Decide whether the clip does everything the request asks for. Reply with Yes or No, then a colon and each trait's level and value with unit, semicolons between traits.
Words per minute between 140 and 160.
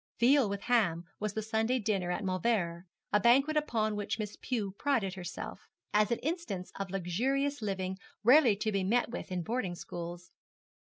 No: average, 170 wpm